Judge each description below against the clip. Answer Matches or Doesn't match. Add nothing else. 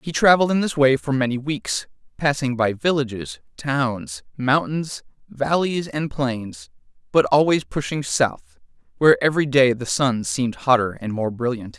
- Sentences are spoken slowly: Doesn't match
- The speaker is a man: Matches